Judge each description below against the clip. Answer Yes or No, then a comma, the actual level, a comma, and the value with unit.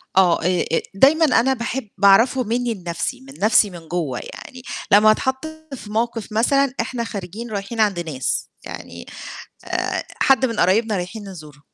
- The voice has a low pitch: No, high, 215 Hz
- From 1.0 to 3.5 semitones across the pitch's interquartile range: No, average, 5.2 semitones